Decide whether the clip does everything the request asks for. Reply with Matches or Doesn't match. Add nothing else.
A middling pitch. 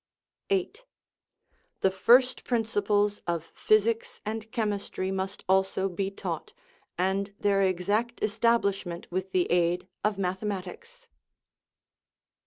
Doesn't match